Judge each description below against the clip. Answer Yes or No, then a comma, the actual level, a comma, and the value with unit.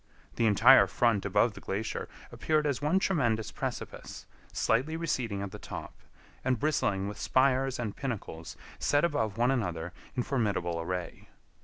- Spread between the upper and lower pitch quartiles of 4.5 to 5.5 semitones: Yes, average, 5.2 semitones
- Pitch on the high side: No, low, 115 Hz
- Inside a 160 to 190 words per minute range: No, average, 150 wpm